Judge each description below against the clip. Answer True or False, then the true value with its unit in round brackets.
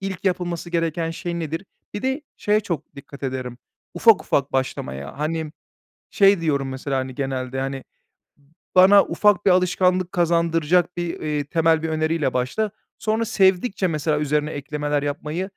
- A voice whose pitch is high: False (165 Hz)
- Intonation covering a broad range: False (4.2 semitones)